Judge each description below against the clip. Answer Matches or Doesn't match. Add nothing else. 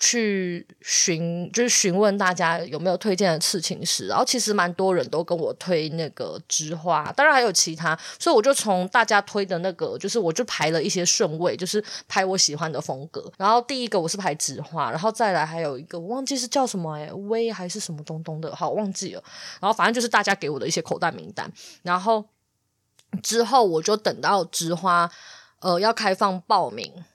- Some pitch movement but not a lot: Matches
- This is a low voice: Doesn't match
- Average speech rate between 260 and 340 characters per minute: Matches